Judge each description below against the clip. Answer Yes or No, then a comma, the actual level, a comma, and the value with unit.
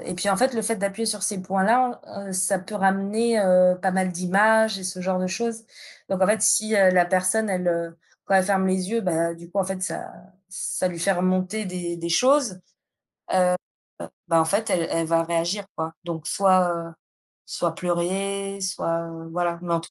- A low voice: No, medium, 185 Hz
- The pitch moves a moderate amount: No, narrow, 2.3 semitones